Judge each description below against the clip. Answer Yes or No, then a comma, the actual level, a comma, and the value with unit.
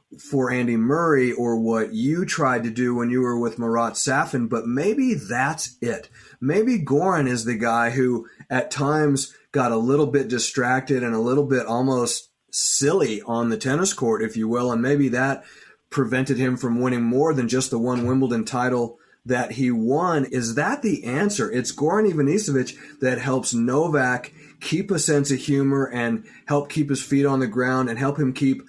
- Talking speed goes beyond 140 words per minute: Yes, average, 185 wpm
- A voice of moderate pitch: No, low, 130 Hz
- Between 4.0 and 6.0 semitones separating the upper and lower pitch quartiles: No, average, 2.8 semitones